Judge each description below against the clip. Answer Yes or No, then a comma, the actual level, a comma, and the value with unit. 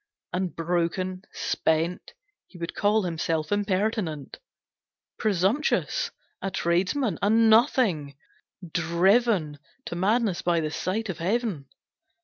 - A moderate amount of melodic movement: Yes, average, 4.3 semitones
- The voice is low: No, medium, 185 Hz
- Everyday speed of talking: No, slow, 105 wpm